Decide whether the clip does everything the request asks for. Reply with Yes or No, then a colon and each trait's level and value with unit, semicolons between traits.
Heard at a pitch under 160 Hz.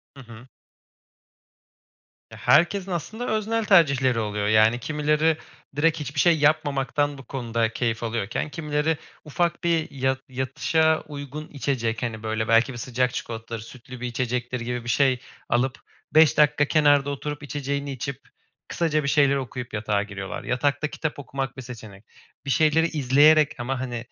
Yes: low, 135 Hz